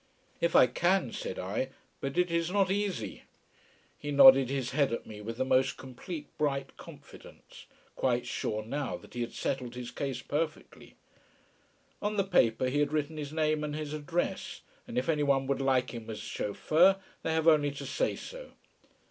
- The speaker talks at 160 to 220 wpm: Yes, average, 180 wpm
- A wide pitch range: No, average, 4.1 semitones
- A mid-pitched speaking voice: Yes, medium, 145 Hz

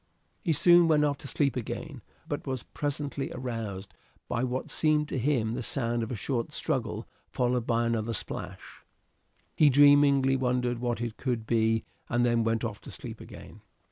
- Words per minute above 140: Yes, average, 175 wpm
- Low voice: Yes, low, 125 Hz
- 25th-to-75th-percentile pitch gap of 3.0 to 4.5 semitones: Yes, average, 3.4 semitones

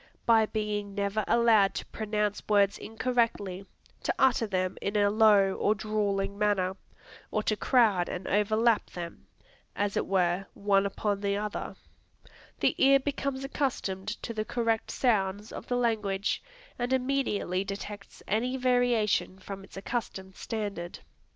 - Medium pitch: No, high, 210 Hz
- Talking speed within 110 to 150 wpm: Yes, average, 140 wpm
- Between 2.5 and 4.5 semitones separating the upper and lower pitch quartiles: Yes, average, 2.8 semitones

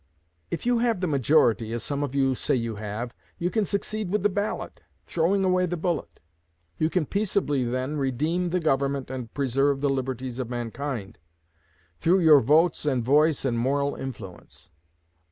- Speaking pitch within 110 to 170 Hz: Yes, medium, 140 Hz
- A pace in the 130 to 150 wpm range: No, average, 170 wpm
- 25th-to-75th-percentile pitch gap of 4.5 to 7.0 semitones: Yes, wide, 5.6 semitones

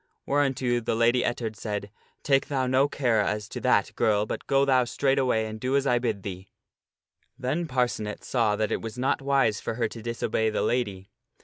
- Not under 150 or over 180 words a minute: No, average, 200 wpm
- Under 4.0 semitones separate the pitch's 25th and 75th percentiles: Yes, average, 3.5 semitones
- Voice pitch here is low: Yes, low, 120 Hz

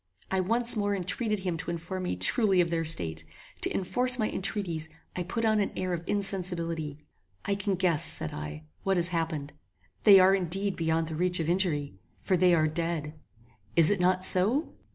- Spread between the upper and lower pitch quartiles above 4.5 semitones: No, average, 3.1 semitones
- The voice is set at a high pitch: No, medium, 180 Hz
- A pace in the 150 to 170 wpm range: No, average, 190 wpm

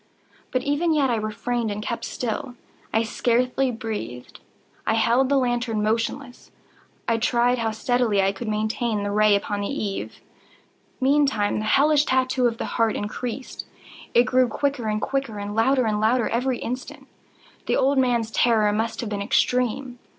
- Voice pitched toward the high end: Yes, high, 235 Hz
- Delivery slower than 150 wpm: No, average, 165 wpm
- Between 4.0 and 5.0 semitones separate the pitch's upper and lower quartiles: No, average, 3.0 semitones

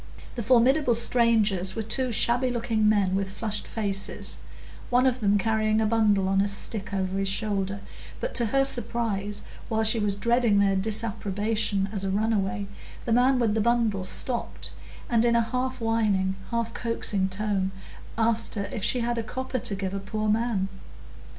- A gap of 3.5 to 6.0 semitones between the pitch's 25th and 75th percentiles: No, average, 2.9 semitones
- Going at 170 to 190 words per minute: Yes, average, 175 wpm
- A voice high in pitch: Yes, high, 220 Hz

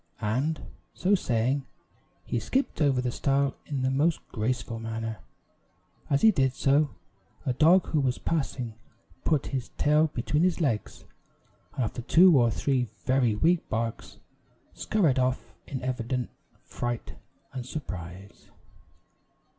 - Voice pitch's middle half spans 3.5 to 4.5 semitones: Yes, average, 4.1 semitones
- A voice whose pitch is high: No, low, 130 Hz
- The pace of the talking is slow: Yes, slow, 130 wpm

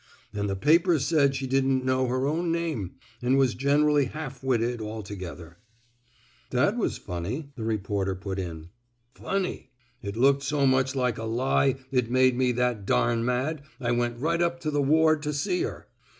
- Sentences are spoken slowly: No, average, 195 wpm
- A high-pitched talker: No, low, 130 Hz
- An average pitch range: Yes, average, 4.1 semitones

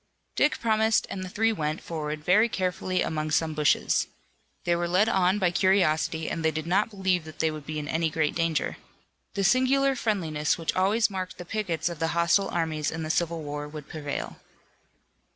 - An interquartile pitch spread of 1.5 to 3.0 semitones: No, average, 3.7 semitones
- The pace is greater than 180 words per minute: Yes, average, 190 wpm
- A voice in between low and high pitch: Yes, medium, 170 Hz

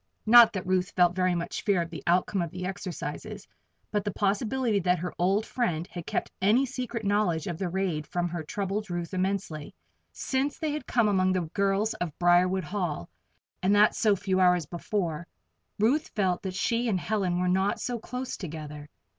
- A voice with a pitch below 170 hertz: No, medium, 185 Hz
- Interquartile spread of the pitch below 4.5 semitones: Yes, average, 3.1 semitones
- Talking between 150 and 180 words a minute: No, average, 190 wpm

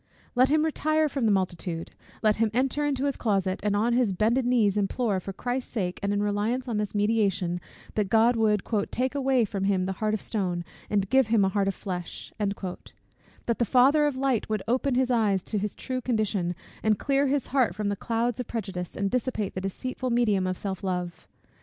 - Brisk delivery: Yes, fast, 210 wpm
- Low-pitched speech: No, high, 215 Hz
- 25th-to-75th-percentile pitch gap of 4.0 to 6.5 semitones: Yes, average, 4.4 semitones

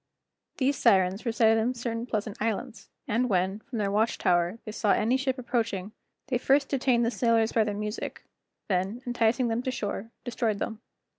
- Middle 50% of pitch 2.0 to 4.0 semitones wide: Yes, average, 2.8 semitones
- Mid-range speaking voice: No, high, 225 Hz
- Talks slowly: No, average, 175 wpm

